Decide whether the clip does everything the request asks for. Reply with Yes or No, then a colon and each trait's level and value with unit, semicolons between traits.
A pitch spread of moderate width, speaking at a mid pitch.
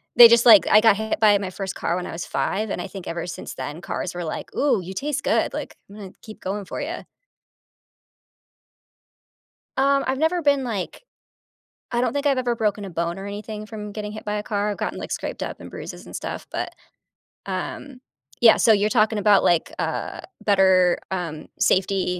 No: average, 3.4 semitones; high, 210 Hz